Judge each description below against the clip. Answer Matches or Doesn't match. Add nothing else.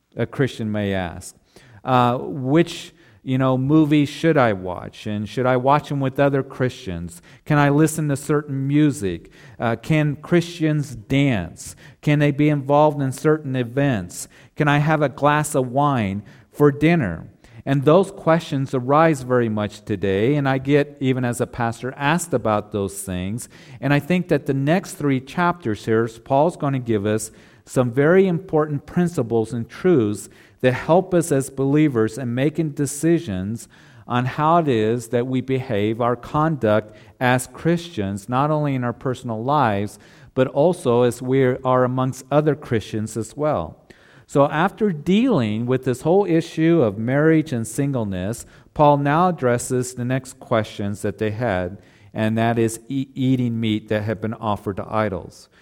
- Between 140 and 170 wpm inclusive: Matches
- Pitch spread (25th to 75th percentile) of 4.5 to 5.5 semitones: Matches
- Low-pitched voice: Matches